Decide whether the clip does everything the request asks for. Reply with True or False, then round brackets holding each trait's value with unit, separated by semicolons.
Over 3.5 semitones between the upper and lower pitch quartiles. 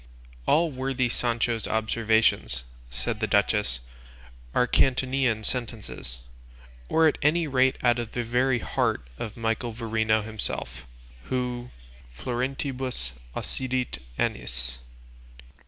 False (3.0 semitones)